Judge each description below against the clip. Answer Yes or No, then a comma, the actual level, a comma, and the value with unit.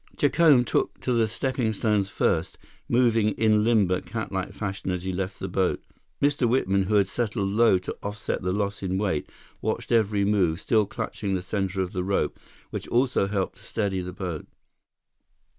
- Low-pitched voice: Yes, low, 100 Hz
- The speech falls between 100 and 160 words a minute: No, average, 175 wpm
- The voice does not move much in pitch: No, average, 3.0 semitones